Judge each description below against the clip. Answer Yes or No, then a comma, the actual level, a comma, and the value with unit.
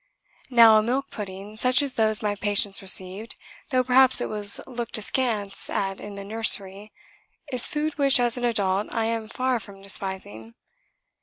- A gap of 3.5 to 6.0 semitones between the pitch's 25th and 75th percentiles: Yes, average, 3.8 semitones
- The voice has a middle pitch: No, high, 215 Hz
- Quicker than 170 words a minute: No, average, 165 wpm